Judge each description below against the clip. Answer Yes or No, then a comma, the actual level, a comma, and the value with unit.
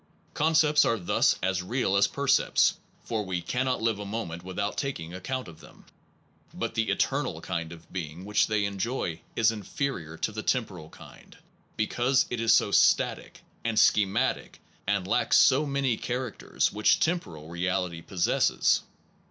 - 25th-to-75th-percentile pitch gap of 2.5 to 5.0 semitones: No, wide, 5.5 semitones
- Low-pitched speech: Yes, low, 105 Hz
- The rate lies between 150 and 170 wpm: Yes, average, 160 wpm